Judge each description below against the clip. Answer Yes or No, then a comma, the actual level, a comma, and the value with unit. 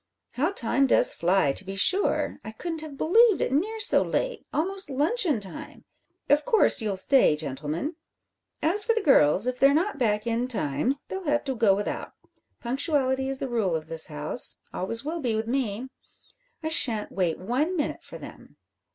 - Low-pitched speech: No, very high, 260 Hz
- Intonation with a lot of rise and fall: Yes, wide, 7.5 semitones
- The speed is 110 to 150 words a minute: No, average, 180 wpm